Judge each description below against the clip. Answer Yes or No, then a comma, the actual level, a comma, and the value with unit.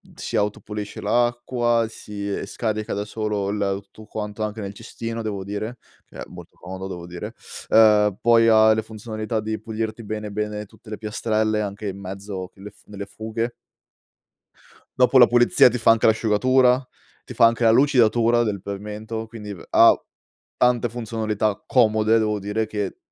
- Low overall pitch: Yes, low, 110 Hz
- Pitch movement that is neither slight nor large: No, narrow, 1.8 semitones